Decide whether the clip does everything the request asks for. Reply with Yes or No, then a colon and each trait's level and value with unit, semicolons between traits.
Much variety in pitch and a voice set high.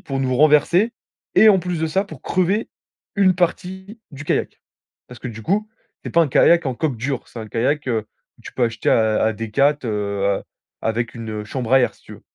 No: wide, 7.4 semitones; low, 135 Hz